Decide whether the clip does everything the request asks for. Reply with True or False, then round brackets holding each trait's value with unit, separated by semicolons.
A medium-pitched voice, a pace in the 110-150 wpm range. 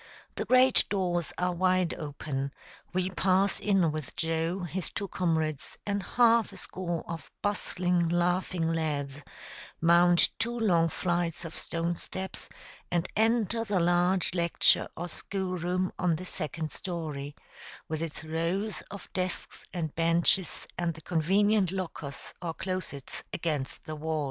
True (175 Hz; 140 wpm)